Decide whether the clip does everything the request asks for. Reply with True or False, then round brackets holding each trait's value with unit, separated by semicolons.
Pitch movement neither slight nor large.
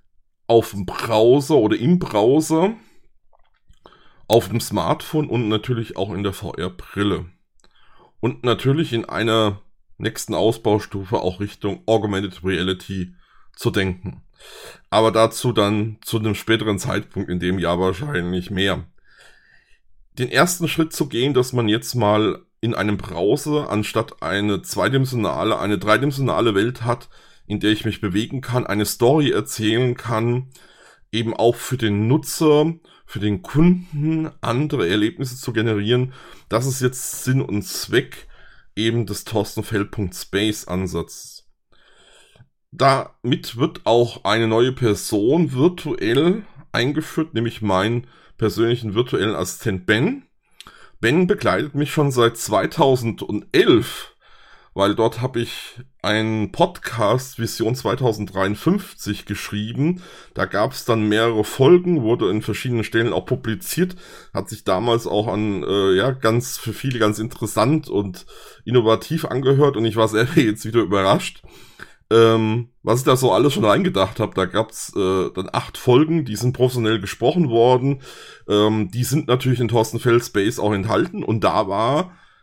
True (3.6 semitones)